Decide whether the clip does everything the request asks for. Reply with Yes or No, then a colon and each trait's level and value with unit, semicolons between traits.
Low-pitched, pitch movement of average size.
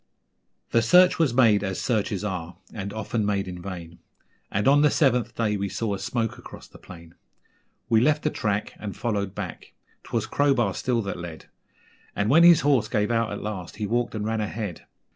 Yes: low, 105 Hz; average, 3.3 semitones